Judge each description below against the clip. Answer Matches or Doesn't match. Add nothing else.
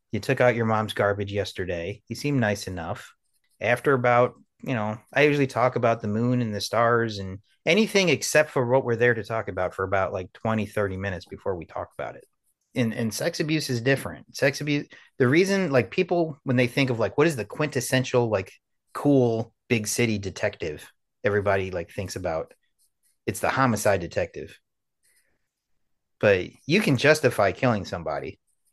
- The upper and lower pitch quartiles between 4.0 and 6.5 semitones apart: Matches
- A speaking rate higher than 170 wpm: Matches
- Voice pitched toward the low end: Matches